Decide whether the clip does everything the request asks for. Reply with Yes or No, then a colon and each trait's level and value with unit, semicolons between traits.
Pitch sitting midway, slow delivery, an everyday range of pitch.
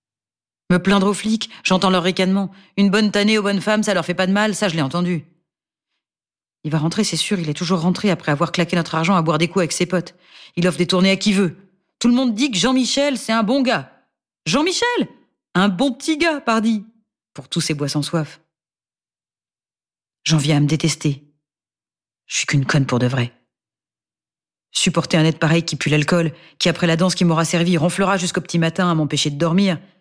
No: medium, 180 Hz; average, 215 wpm; average, 3.8 semitones